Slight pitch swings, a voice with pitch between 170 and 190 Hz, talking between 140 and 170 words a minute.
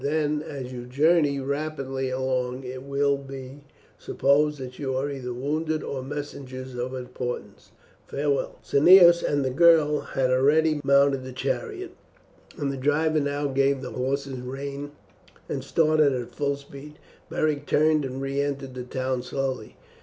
No: narrow, 2.2 semitones; medium, 140 Hz; average, 150 wpm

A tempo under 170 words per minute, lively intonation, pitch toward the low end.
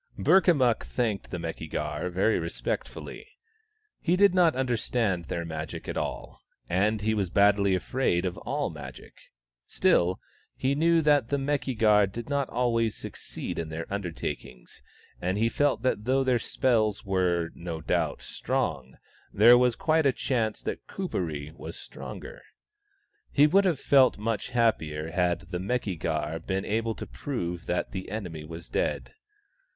Yes: average, 155 wpm; wide, 6.7 semitones; low, 105 Hz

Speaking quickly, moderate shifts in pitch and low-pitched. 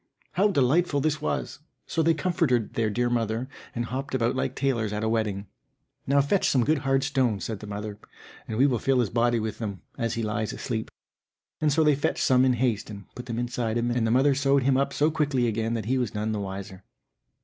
Yes: fast, 230 wpm; average, 3.9 semitones; low, 120 Hz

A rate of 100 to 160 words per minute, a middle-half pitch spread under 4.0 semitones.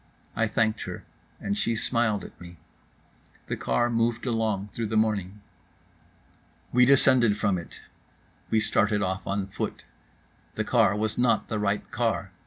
Yes: average, 150 wpm; narrow, 2.4 semitones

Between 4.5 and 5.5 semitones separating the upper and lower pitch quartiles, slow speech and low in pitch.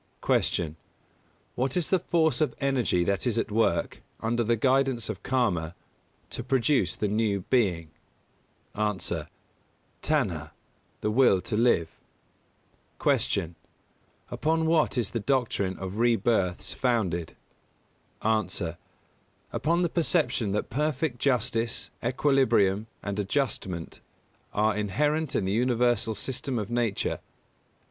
Yes: average, 5.1 semitones; slow, 120 wpm; low, 115 Hz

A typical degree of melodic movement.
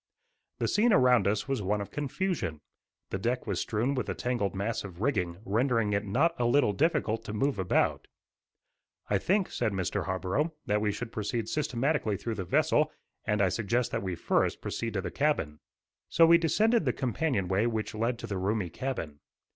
No: wide, 5.7 semitones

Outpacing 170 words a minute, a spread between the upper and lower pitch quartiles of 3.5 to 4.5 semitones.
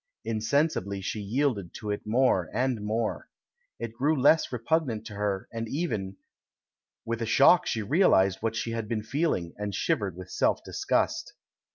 No: average, 160 wpm; average, 4.2 semitones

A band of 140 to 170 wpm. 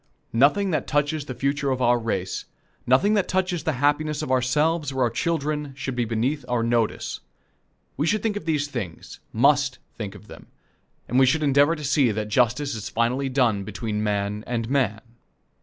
No: average, 185 wpm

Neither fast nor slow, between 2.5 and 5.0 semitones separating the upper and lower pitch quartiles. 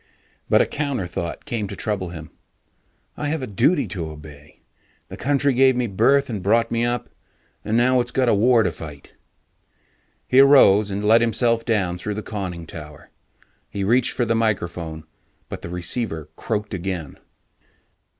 No: average, 170 wpm; wide, 5.6 semitones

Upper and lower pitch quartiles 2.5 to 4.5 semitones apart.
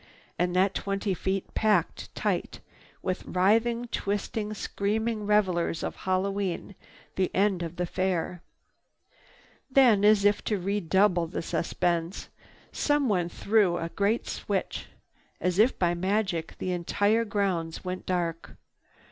Yes: average, 2.8 semitones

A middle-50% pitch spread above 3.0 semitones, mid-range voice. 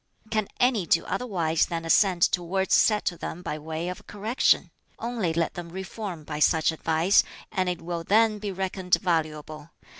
Yes: average, 3.5 semitones; medium, 180 Hz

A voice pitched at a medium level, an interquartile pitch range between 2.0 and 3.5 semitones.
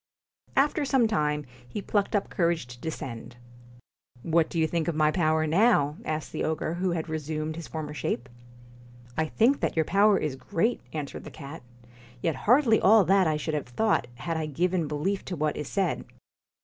No: medium, 160 Hz; average, 4.1 semitones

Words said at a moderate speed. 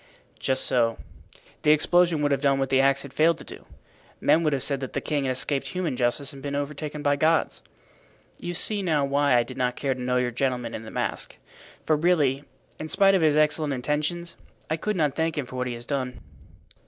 No: fast, 225 wpm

